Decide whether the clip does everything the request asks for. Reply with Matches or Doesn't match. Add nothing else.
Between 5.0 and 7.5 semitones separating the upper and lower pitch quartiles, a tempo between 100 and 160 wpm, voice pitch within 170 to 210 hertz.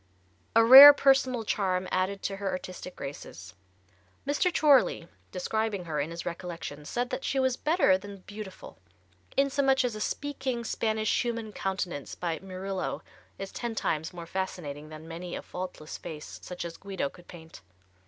Matches